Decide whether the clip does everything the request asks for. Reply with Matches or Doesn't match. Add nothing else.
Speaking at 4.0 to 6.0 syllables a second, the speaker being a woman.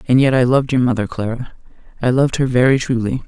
Doesn't match